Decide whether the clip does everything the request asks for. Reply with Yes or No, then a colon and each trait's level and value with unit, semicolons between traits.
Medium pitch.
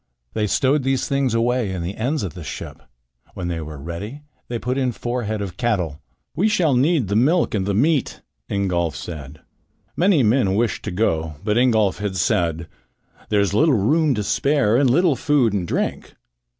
No: low, 110 Hz